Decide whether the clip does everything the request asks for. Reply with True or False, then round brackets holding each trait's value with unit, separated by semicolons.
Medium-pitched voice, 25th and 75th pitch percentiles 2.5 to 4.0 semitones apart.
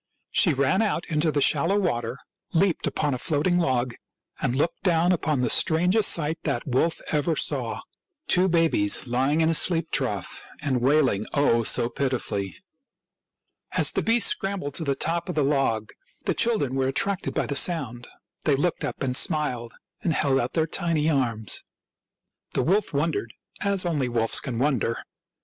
False (150 Hz; 4.8 semitones)